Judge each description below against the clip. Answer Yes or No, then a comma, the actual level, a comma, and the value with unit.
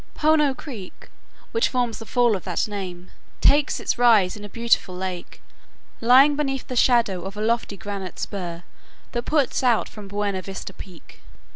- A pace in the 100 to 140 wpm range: No, average, 165 wpm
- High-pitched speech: Yes, high, 215 Hz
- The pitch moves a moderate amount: Yes, average, 4.6 semitones